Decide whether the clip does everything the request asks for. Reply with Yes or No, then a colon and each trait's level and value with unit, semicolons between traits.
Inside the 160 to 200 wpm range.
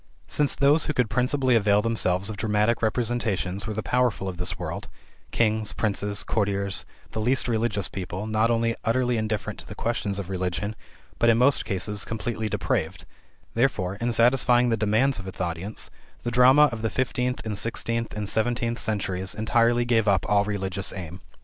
Yes: average, 175 wpm